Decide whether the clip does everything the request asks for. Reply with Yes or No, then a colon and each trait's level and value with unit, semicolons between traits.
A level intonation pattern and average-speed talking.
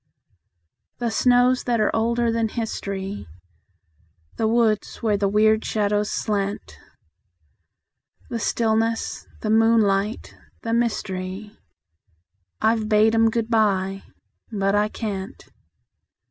No: narrow, 2.0 semitones; slow, 105 wpm